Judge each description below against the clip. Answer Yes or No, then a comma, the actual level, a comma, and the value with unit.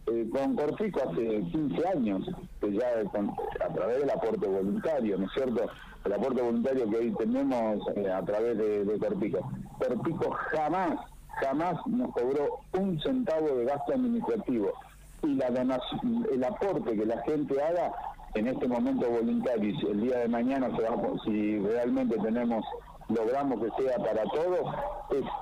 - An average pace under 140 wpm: No, average, 160 wpm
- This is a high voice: No, low, 135 Hz